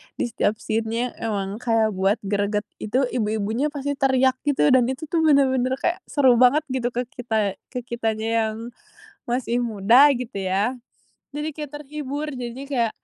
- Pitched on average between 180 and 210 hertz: No, high, 245 Hz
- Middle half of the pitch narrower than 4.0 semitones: Yes, average, 3.5 semitones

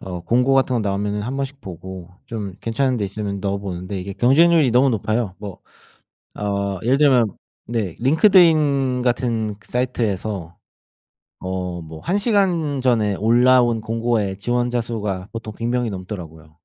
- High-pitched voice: No, low, 115 Hz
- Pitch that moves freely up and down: No, average, 4.4 semitones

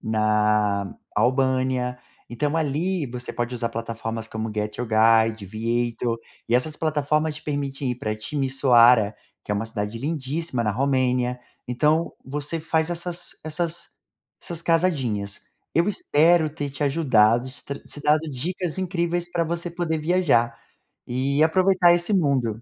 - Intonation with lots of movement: Yes, wide, 5.7 semitones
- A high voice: No, low, 135 Hz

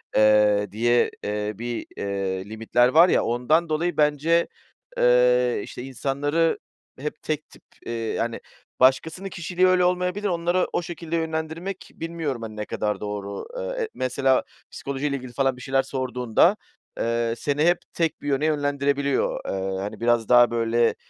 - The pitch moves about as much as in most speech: No, wide, 5.7 semitones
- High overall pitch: No, low, 135 Hz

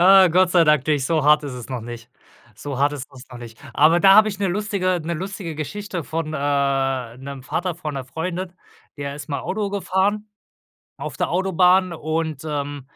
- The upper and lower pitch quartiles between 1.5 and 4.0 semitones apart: No, average, 4.9 semitones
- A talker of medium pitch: Yes, medium, 155 Hz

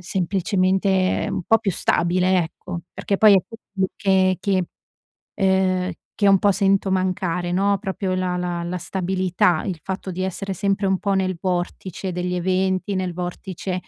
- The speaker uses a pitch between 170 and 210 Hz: Yes, medium, 185 Hz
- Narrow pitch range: Yes, narrow, 1.2 semitones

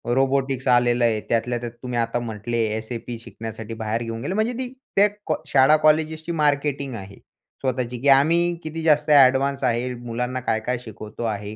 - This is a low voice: Yes, low, 125 Hz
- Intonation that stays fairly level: No, average, 3.7 semitones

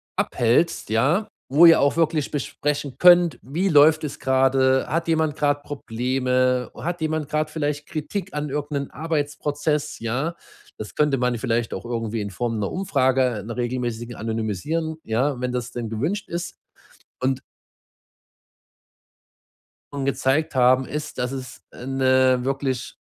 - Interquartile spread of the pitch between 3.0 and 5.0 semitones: Yes, average, 3.6 semitones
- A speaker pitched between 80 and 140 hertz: Yes, low, 135 Hz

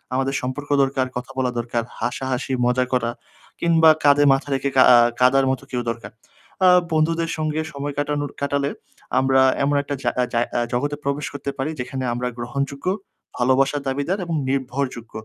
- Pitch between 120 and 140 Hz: Yes, low, 135 Hz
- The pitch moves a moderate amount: No, narrow, 2.2 semitones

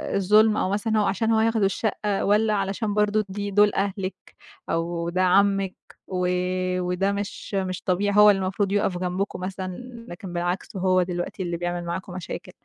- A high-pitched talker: Yes, high, 195 Hz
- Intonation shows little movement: Yes, narrow, 2.1 semitones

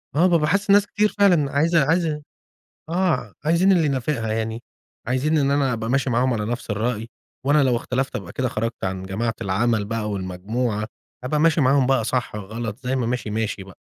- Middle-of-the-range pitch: No, low, 125 Hz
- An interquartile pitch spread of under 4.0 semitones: No, average, 5.2 semitones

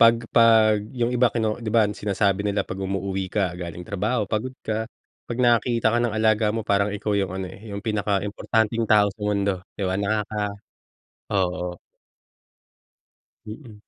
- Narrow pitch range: Yes, narrow, 2.2 semitones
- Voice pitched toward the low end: Yes, low, 105 Hz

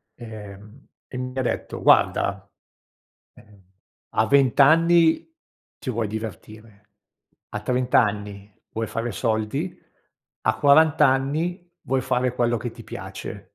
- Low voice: Yes, low, 120 Hz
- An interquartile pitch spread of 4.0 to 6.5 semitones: Yes, average, 4.3 semitones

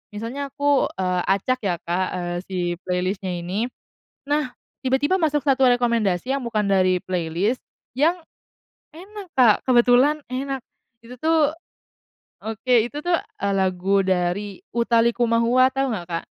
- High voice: Yes, high, 235 Hz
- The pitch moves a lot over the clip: Yes, wide, 6.3 semitones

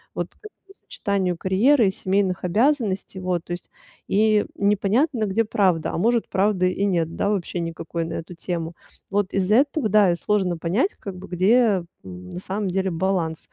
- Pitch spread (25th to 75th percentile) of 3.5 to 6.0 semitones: No, average, 3.1 semitones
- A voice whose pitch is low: No, high, 190 Hz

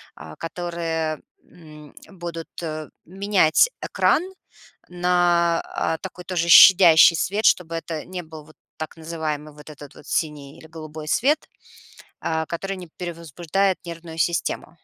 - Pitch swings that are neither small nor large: No, narrow, 2.1 semitones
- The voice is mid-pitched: Yes, medium, 165 Hz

